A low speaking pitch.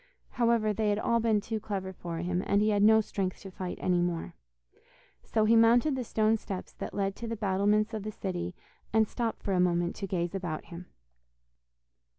No: high, 205 Hz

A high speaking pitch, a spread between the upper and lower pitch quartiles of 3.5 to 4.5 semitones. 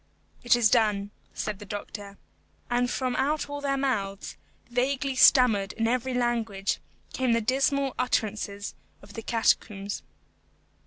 Yes: high, 235 Hz; average, 3.9 semitones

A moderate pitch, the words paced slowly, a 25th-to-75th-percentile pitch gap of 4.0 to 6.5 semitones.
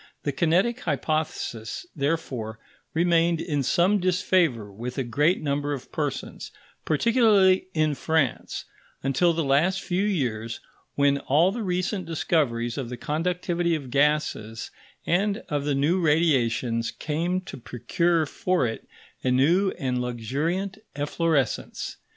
Yes: medium, 155 Hz; slow, 125 wpm; average, 5.0 semitones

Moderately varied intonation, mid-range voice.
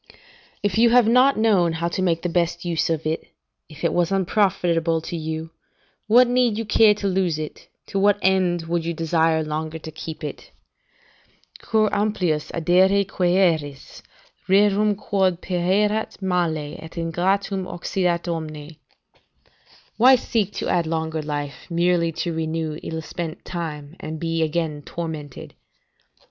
Yes: average, 3.3 semitones; medium, 170 Hz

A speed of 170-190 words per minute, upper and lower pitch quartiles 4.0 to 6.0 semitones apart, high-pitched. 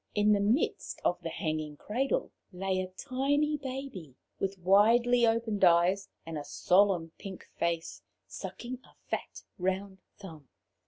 No: average, 140 wpm; average, 5.2 semitones; high, 195 Hz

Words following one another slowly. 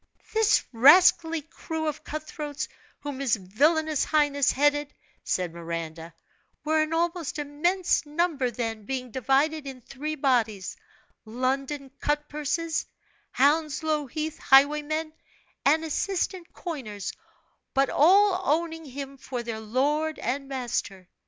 Yes: slow, 120 wpm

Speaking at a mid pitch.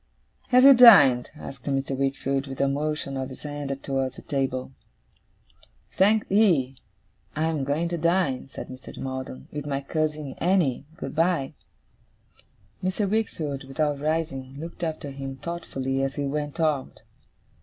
Yes: medium, 145 Hz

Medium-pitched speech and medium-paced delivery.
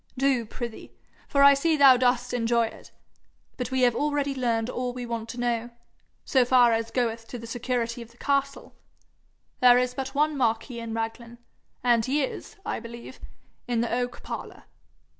No: high, 245 Hz; average, 180 wpm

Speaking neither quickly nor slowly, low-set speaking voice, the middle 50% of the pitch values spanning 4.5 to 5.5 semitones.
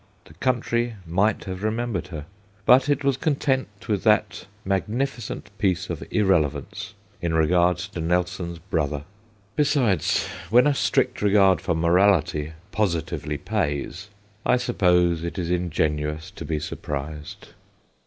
No: slow, 130 wpm; very low, 90 Hz; average, 5.1 semitones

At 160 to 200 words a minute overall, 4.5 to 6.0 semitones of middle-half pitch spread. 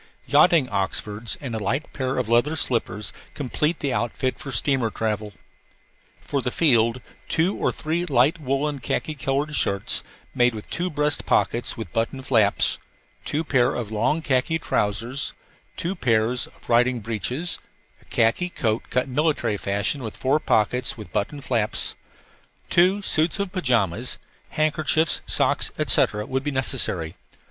No: average, 145 wpm; average, 5.0 semitones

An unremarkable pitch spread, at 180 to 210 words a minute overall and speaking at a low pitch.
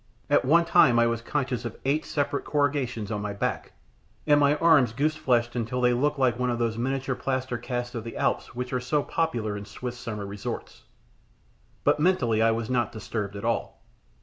Yes: average, 3.4 semitones; average, 200 wpm; low, 125 Hz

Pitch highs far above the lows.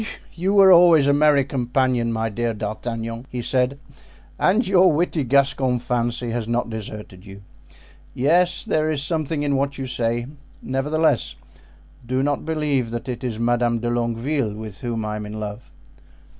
No: average, 3.9 semitones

